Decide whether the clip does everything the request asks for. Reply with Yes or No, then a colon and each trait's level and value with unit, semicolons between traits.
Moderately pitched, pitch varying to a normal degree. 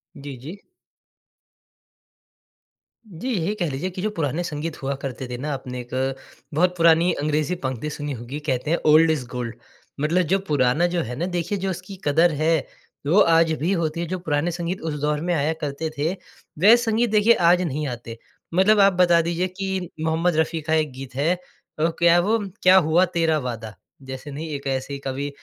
Yes: medium, 160 Hz; average, 4.1 semitones